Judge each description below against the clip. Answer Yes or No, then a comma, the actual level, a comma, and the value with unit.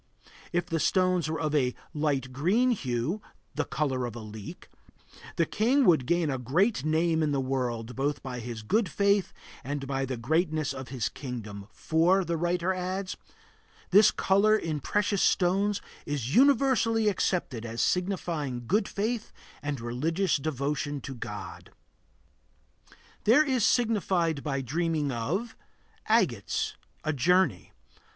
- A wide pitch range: Yes, wide, 6.3 semitones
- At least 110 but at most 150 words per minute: Yes, average, 140 wpm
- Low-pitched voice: No, medium, 155 Hz